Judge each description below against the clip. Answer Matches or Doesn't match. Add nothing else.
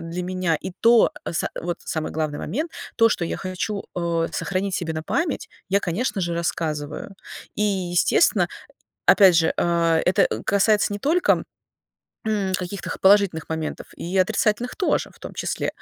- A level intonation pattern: Doesn't match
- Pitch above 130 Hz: Matches